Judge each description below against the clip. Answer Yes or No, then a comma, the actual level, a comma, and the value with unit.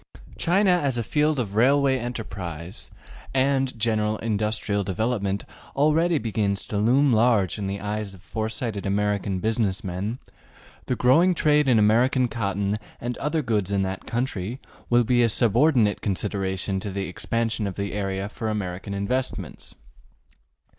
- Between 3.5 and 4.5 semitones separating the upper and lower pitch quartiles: Yes, average, 4.0 semitones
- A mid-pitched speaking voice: No, low, 110 Hz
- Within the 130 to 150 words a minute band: Yes, average, 145 wpm